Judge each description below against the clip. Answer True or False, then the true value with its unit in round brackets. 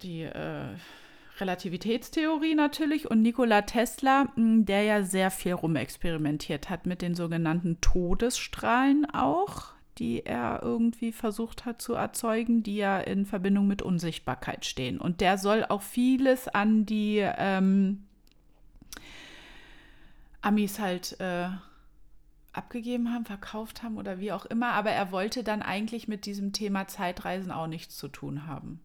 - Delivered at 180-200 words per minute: False (135 wpm)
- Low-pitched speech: False (205 Hz)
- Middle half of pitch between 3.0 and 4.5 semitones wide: True (4.1 semitones)